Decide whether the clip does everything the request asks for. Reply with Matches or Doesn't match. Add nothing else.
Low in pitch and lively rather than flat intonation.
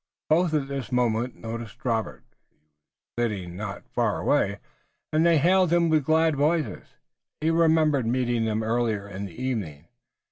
Matches